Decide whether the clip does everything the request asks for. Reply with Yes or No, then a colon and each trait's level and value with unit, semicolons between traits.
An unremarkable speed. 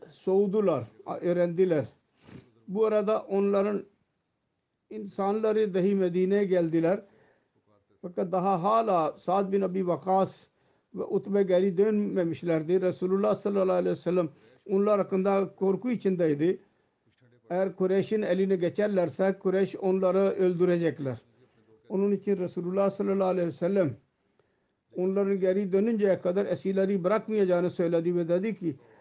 Yes: average, 110 wpm